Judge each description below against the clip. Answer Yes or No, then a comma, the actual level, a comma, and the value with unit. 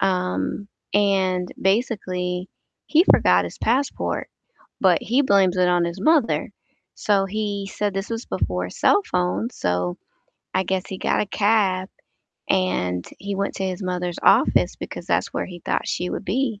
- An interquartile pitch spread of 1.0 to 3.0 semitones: Yes, narrow, 2.5 semitones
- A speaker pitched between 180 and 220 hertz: Yes, high, 190 Hz